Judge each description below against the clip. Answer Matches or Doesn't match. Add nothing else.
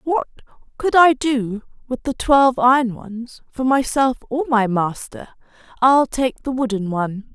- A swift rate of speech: Doesn't match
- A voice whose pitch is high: Matches